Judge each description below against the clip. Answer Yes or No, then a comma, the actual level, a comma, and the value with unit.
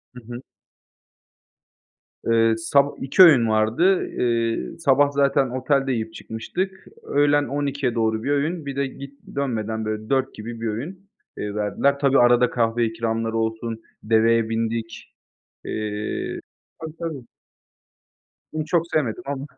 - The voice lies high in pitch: No, low, 120 Hz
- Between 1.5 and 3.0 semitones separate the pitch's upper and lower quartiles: No, average, 4.0 semitones